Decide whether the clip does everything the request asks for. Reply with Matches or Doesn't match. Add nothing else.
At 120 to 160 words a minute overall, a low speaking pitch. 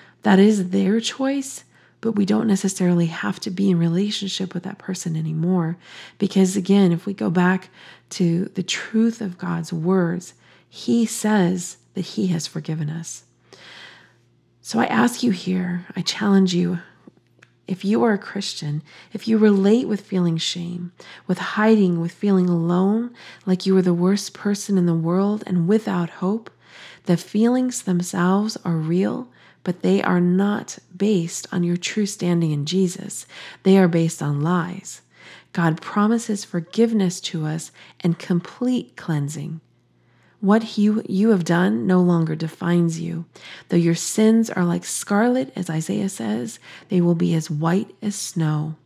Doesn't match